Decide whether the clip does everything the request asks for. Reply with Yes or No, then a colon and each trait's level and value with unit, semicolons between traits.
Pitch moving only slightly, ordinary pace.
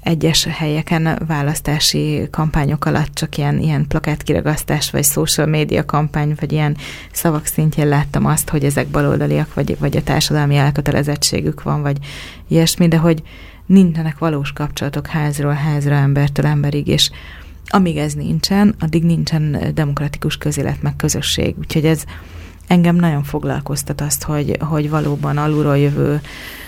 Yes: narrow, 1.6 semitones; average, 135 wpm